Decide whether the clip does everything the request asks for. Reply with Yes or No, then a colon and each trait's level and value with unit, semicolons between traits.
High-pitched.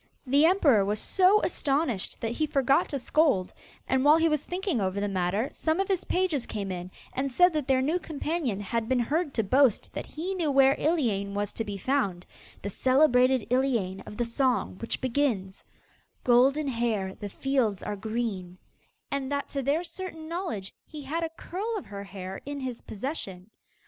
Yes: very high, 260 Hz